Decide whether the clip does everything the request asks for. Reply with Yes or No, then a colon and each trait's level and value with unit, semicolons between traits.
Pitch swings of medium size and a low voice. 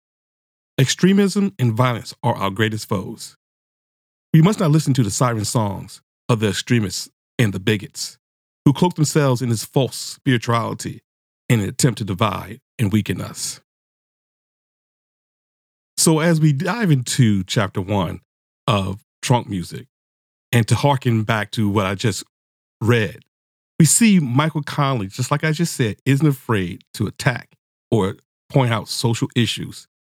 No: wide, 5.9 semitones; low, 120 Hz